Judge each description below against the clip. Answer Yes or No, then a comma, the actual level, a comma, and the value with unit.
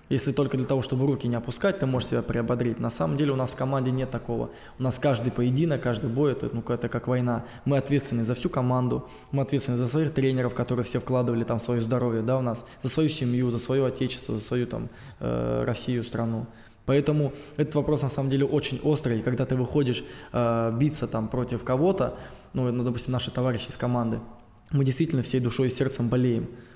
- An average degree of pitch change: No, narrow, 2.3 semitones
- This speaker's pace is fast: Yes, fast, 200 wpm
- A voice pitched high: No, low, 125 Hz